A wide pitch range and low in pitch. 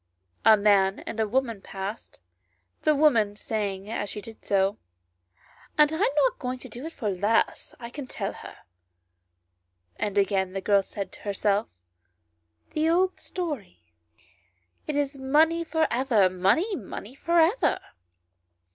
No: wide, 7.2 semitones; high, 215 Hz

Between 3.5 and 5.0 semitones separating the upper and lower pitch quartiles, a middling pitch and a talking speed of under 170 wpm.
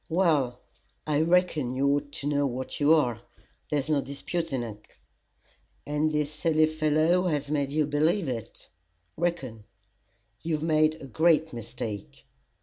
No: average, 2.7 semitones; medium, 150 Hz; average, 140 wpm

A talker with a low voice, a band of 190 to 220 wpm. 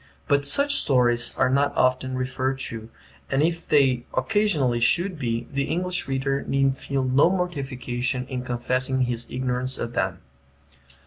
No: low, 130 Hz; average, 145 wpm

